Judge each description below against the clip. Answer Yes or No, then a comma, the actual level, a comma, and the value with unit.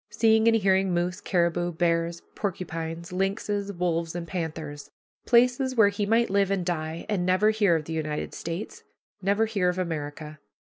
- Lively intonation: No, average, 3.4 semitones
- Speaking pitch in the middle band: Yes, medium, 180 Hz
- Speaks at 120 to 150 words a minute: No, average, 160 wpm